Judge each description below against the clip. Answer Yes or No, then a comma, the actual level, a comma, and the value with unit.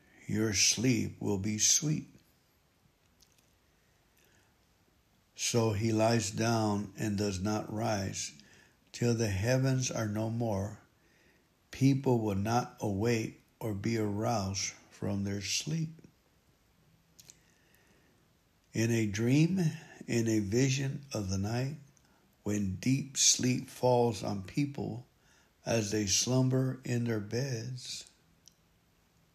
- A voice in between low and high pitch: No, low, 115 Hz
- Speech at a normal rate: No, slow, 100 wpm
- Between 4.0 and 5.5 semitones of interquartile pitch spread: No, average, 3.6 semitones